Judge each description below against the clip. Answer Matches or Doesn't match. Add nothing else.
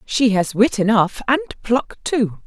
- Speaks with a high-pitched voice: Matches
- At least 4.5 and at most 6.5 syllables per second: Doesn't match